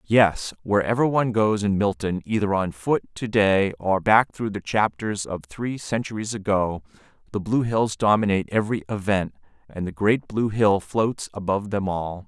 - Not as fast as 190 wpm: Yes, average, 170 wpm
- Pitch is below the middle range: Yes, low, 105 Hz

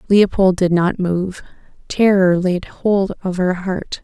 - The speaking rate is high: No, average, 150 wpm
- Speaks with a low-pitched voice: No, medium, 185 Hz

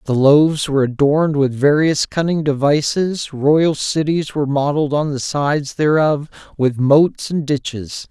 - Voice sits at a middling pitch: Yes, medium, 145 Hz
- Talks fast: No, average, 150 wpm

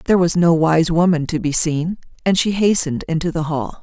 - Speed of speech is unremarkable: No, fast, 220 wpm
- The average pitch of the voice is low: No, medium, 165 Hz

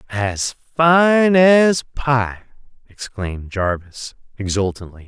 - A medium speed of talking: No, slow, 85 wpm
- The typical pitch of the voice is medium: No, low, 125 Hz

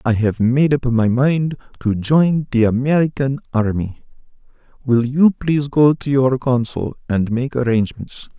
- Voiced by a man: Yes, male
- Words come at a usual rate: Yes, average, 150 wpm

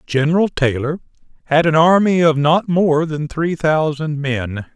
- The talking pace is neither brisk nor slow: Yes, average, 150 wpm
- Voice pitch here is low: No, medium, 155 Hz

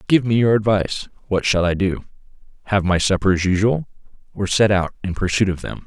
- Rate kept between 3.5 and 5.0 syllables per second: No, 5.8 syllables/s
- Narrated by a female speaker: No, male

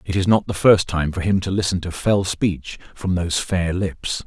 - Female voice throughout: No, male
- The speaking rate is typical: No, fast, 240 wpm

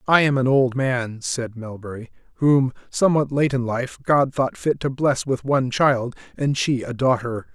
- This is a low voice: Yes, low, 130 Hz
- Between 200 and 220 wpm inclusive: No, average, 190 wpm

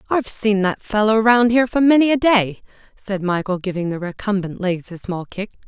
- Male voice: No, female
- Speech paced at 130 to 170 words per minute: No, average, 200 wpm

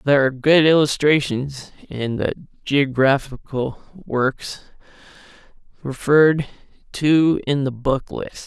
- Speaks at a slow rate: Yes, slow, 100 wpm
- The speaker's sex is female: No, male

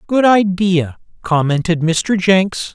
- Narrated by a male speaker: Yes, male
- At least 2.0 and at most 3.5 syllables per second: Yes, 3.4 syllables/s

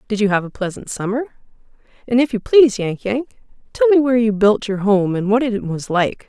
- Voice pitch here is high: Yes, high, 215 Hz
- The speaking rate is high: Yes, fast, 230 wpm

